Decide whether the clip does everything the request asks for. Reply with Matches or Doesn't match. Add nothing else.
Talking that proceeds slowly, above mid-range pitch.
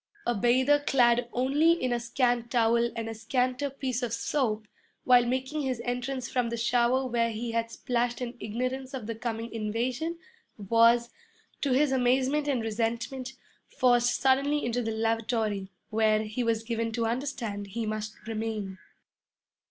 Doesn't match